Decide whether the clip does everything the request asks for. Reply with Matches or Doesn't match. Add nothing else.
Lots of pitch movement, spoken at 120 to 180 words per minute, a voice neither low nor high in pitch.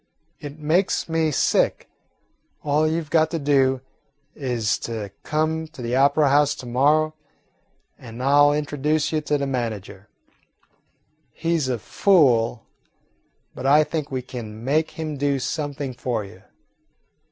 Doesn't match